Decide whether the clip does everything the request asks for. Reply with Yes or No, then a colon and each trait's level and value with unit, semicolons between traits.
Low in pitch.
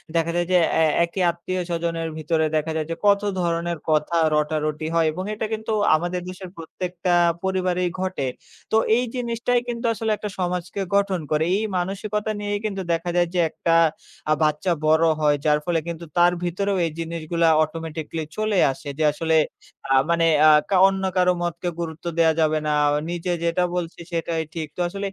No: medium, 170 Hz